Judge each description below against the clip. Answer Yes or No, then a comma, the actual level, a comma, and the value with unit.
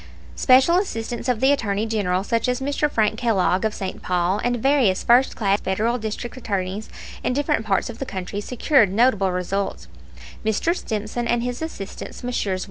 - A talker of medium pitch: No, high, 225 Hz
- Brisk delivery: No, average, 170 wpm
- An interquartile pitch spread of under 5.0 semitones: Yes, average, 4.0 semitones